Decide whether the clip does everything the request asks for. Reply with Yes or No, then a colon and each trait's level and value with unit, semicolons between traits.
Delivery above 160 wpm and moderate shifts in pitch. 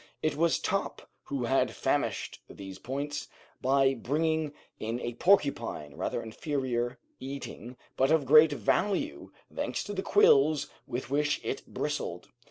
No: slow, 135 wpm; average, 4.0 semitones